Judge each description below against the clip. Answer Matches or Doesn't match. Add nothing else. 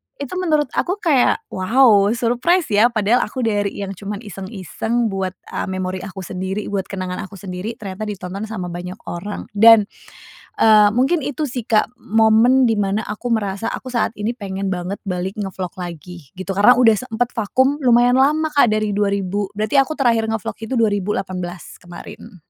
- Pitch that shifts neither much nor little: Matches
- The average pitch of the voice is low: Doesn't match